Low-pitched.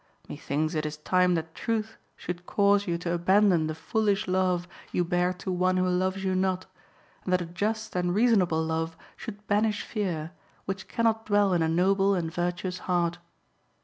No: medium, 185 Hz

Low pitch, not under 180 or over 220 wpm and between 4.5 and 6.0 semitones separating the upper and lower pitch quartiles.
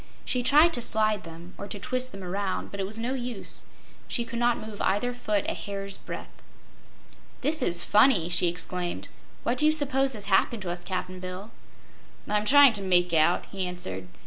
No: high, 205 Hz; average, 195 wpm; average, 5.1 semitones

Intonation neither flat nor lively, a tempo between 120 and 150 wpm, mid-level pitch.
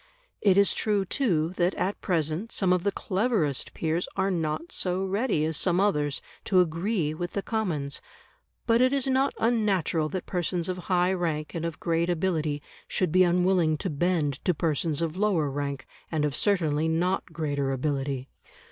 No: average, 3.8 semitones; average, 175 wpm; medium, 175 Hz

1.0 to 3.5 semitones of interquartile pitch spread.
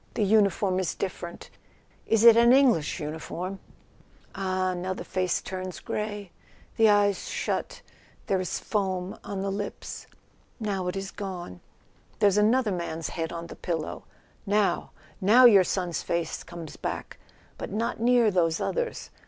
Yes: average, 2.9 semitones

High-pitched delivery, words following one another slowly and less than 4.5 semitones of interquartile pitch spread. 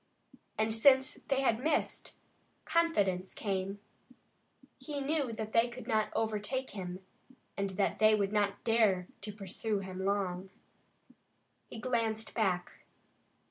Yes: high, 215 Hz; slow, 120 wpm; average, 3.4 semitones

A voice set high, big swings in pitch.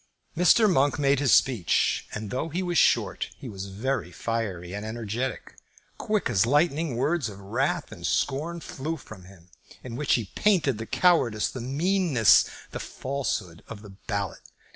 No: low, 125 Hz; wide, 6.4 semitones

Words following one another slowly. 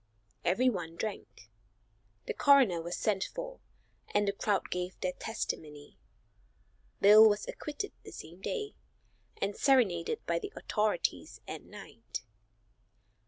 Yes: slow, 120 wpm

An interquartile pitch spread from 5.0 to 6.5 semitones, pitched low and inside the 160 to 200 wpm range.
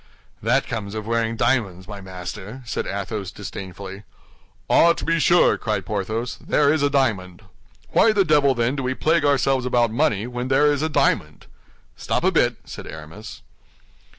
Yes: wide, 5.6 semitones; low, 120 Hz; average, 170 wpm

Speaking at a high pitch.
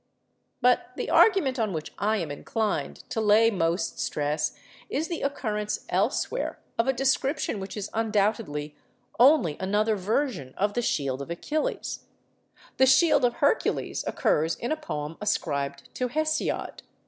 Yes: high, 215 Hz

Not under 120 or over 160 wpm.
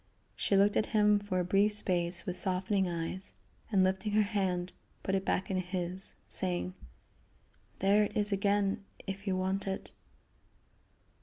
Yes: average, 155 wpm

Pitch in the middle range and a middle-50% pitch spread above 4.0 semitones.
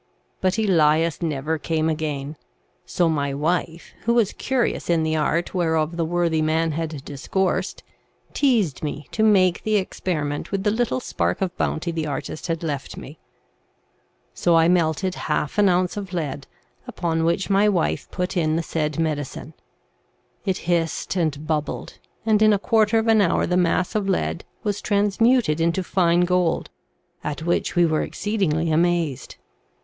No: medium, 170 Hz; average, 3.4 semitones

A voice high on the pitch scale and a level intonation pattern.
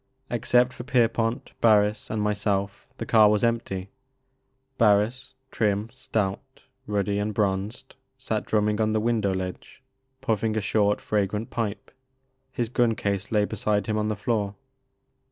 No: low, 105 Hz; narrow, 2.0 semitones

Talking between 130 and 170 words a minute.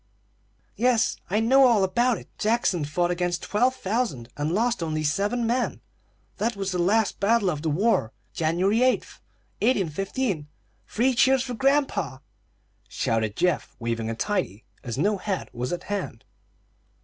Yes: average, 150 wpm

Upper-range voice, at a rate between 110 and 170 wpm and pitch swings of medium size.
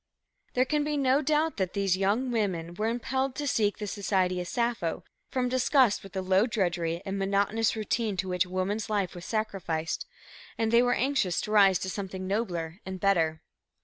No: high, 200 Hz; average, 185 wpm; average, 4.2 semitones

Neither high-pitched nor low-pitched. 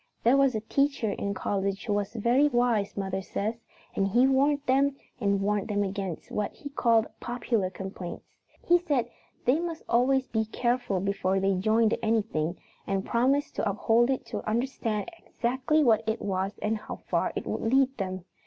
No: high, 225 Hz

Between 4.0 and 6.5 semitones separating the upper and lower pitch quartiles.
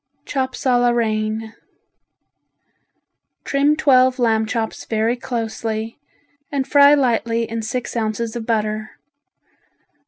No: narrow, 2.5 semitones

